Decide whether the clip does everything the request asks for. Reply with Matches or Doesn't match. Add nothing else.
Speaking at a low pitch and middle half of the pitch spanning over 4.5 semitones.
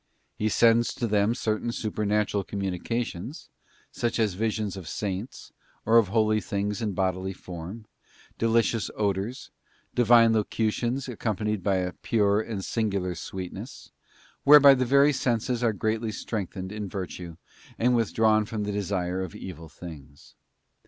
Doesn't match